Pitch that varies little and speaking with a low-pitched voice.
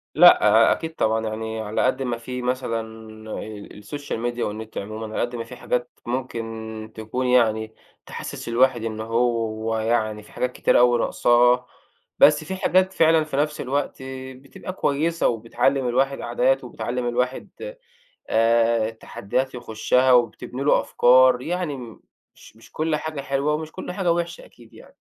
No: average, 3.4 semitones; low, 125 Hz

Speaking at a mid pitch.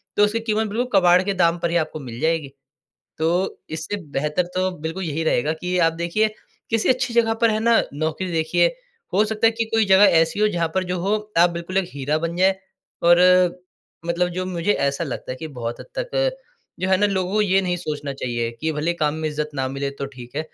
Yes: medium, 175 Hz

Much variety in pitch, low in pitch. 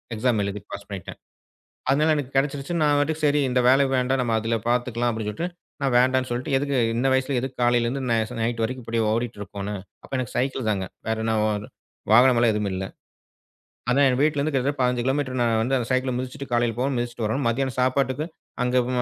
No: average, 2.8 semitones; low, 125 Hz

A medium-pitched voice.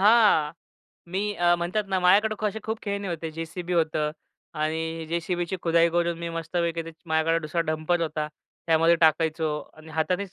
Yes: medium, 170 Hz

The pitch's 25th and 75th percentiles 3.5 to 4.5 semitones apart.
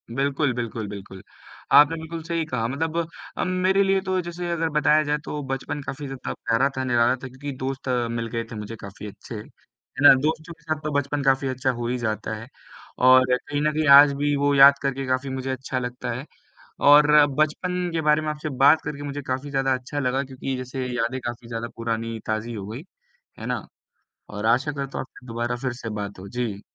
Yes: average, 3.8 semitones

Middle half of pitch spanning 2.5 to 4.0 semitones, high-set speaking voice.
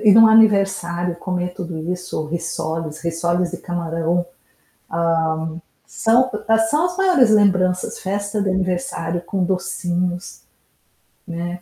No: average, 2.8 semitones; medium, 180 Hz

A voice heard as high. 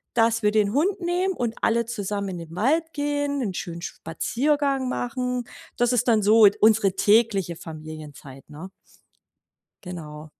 Yes: high, 220 Hz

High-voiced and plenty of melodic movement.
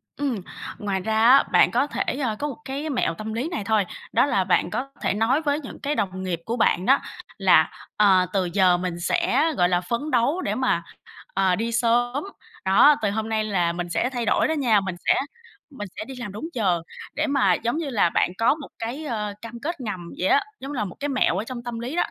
Yes: high, 230 Hz; wide, 6.0 semitones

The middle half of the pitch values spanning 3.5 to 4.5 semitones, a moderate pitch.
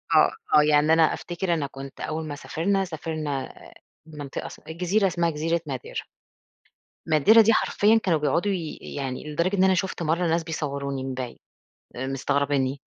Yes: average, 4.0 semitones; medium, 160 Hz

